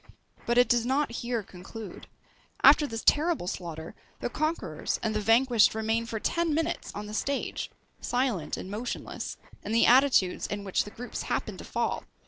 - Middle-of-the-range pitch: No, high, 230 Hz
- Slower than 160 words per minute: No, average, 170 wpm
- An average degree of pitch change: Yes, average, 4.3 semitones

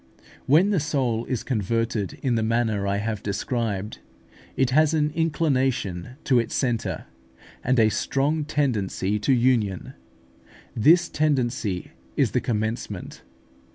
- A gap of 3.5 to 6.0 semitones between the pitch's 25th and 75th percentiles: Yes, average, 4.7 semitones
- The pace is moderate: No, slow, 125 wpm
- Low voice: Yes, low, 120 Hz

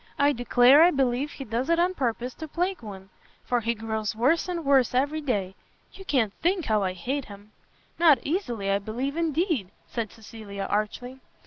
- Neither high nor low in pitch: No, very high, 250 Hz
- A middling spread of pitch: No, wide, 5.9 semitones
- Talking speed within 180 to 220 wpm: Yes, average, 185 wpm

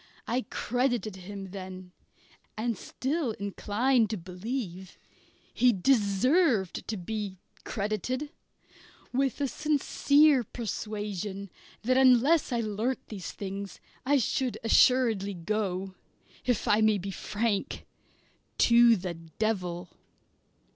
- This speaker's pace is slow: Yes, slow, 105 wpm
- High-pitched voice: Yes, high, 215 Hz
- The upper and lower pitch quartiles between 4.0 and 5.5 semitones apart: Yes, average, 4.5 semitones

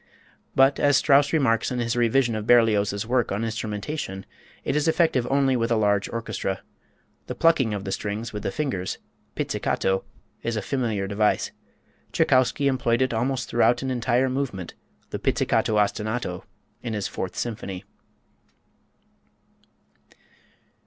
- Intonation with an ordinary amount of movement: Yes, average, 4.0 semitones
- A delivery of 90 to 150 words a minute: Yes, average, 140 wpm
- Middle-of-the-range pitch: No, low, 115 Hz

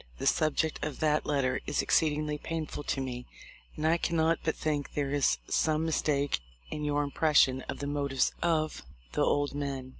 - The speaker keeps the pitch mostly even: Yes, narrow, 1.8 semitones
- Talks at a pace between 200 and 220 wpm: No, average, 185 wpm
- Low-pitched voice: No, medium, 150 Hz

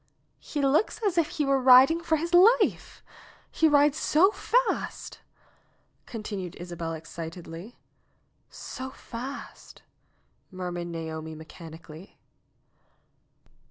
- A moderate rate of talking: No, slow, 105 wpm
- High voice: Yes, high, 240 Hz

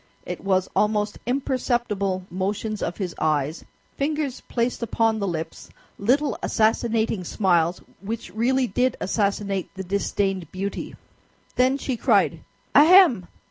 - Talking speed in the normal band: No, slow, 120 wpm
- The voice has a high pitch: Yes, high, 210 Hz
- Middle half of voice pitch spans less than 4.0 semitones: No, average, 4.6 semitones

